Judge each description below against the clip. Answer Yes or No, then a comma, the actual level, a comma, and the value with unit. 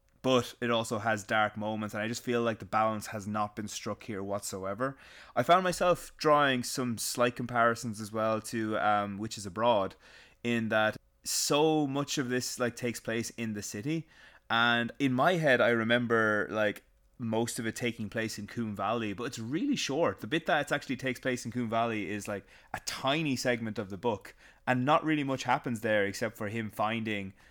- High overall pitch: No, low, 115 Hz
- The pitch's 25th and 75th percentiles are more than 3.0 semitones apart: No, average, 2.7 semitones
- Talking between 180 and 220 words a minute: Yes, average, 200 wpm